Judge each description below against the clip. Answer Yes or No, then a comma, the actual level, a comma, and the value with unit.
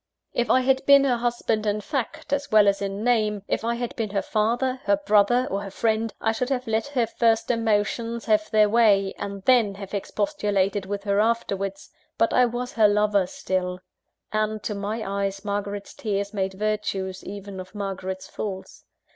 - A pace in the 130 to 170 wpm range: No, average, 185 wpm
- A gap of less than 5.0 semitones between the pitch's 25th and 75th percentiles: Yes, average, 2.7 semitones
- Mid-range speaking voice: No, high, 210 Hz